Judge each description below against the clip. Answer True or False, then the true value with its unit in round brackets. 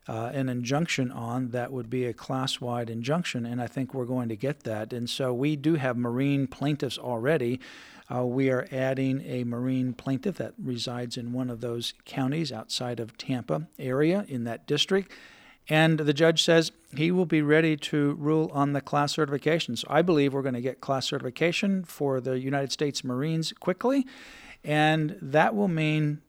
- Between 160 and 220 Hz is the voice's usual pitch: False (135 Hz)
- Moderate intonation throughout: True (3.8 semitones)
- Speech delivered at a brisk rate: False (185 wpm)